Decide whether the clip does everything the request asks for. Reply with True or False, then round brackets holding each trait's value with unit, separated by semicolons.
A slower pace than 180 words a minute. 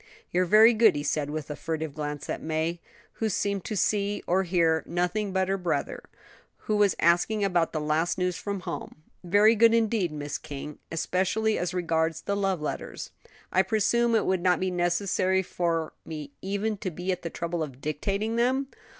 False (185 wpm)